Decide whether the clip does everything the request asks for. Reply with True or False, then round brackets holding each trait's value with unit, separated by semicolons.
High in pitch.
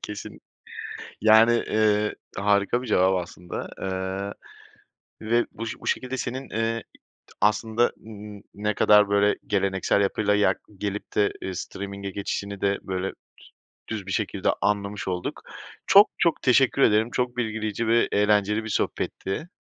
False (105 Hz)